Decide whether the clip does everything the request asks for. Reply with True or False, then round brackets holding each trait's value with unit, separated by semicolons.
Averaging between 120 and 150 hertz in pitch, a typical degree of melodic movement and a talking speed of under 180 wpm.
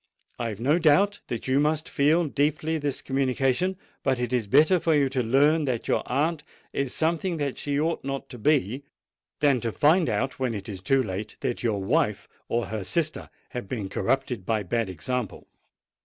False (135 Hz; 4.6 semitones; 185 wpm)